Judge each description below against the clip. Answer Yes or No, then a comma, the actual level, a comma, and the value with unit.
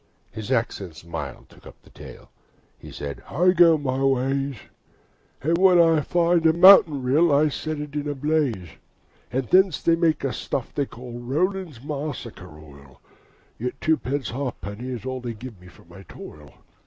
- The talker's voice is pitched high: No, low, 135 Hz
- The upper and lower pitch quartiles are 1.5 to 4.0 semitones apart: No, average, 5.3 semitones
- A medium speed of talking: Yes, average, 170 wpm